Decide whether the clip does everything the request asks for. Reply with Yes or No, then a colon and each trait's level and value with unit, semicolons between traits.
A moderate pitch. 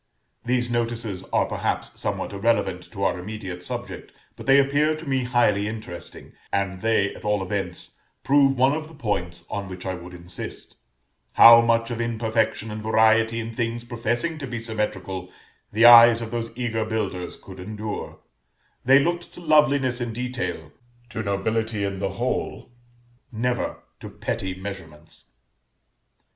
No: low, 110 Hz